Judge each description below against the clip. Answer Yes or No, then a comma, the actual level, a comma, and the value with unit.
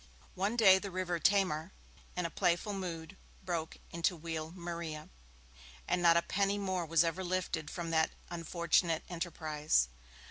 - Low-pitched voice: No, medium, 170 Hz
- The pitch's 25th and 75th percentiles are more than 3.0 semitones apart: No, narrow, 2.4 semitones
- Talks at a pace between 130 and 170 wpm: Yes, average, 145 wpm